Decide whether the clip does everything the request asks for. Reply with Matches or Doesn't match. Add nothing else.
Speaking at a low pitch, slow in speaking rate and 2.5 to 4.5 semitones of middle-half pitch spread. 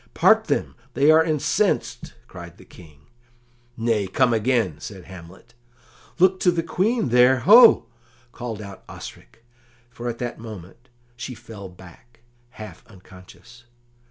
Doesn't match